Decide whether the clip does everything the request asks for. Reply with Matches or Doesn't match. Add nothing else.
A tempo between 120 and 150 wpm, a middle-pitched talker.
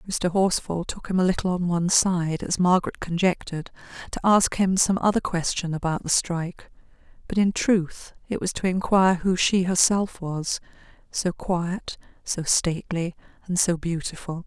Doesn't match